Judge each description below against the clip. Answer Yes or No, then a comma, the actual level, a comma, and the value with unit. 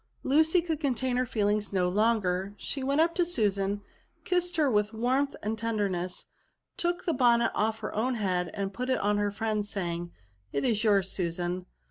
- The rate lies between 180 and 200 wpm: Yes, average, 195 wpm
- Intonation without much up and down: No, average, 5.0 semitones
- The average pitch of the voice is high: Yes, high, 215 Hz